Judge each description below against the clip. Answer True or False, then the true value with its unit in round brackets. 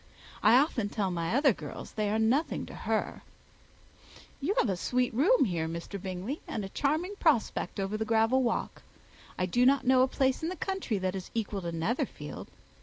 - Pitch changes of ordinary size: False (5.8 semitones)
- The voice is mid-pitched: False (225 Hz)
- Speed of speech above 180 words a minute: True (190 wpm)